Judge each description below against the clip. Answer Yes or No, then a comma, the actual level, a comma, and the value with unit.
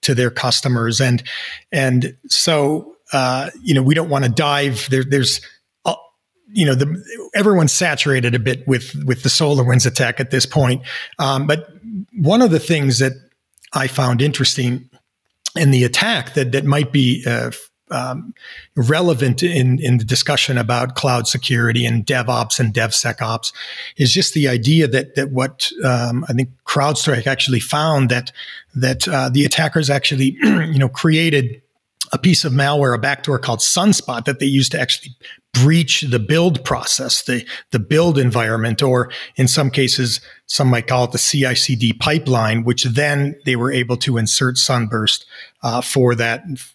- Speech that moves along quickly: No, average, 165 wpm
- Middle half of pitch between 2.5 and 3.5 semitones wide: Yes, average, 2.8 semitones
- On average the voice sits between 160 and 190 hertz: No, low, 135 Hz